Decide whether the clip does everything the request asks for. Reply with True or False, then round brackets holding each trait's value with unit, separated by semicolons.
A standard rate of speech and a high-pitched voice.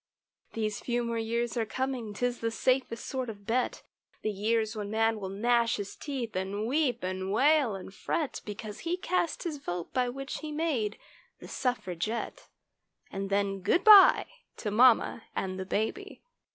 True (165 wpm; 230 Hz)